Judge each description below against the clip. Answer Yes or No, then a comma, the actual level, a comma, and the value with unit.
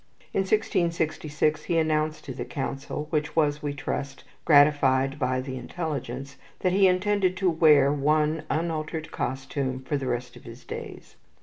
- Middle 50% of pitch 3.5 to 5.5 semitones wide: No, average, 3.0 semitones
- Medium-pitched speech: Yes, medium, 150 Hz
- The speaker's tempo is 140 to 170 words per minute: Yes, average, 150 wpm